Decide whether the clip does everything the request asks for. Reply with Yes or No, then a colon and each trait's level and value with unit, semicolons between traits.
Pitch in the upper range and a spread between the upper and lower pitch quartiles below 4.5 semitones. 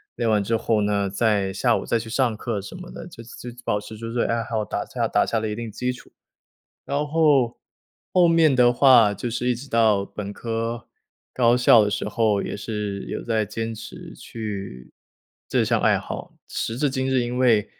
No: low, 115 Hz; average, 2.8 semitones